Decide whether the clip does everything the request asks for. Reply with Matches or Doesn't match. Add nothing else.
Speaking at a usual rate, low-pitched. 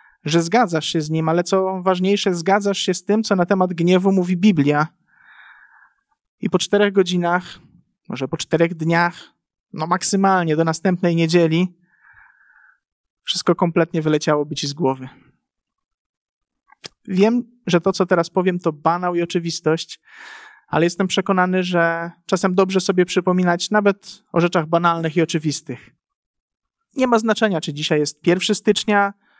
Doesn't match